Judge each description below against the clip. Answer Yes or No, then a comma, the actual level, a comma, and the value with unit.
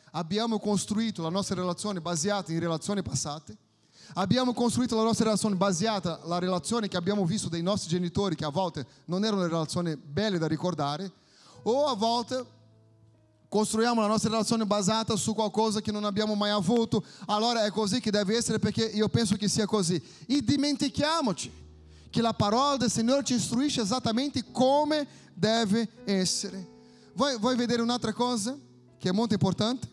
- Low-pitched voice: No, high, 210 Hz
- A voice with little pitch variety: No, average, 4.5 semitones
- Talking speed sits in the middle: Yes, average, 160 wpm